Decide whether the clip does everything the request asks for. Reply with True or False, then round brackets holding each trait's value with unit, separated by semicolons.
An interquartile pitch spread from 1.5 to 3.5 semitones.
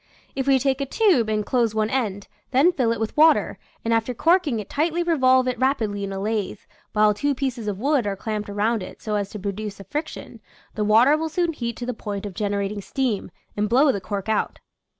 False (4.7 semitones)